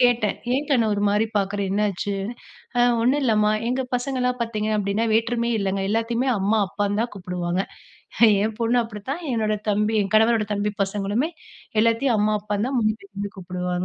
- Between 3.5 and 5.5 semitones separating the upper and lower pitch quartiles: No, narrow, 2.6 semitones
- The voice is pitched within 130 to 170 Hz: No, high, 215 Hz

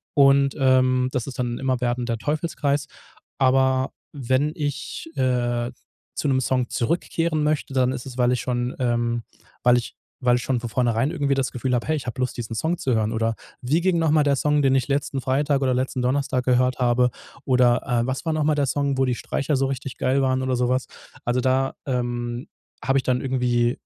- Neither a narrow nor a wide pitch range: No, narrow, 2.1 semitones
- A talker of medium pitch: No, low, 130 Hz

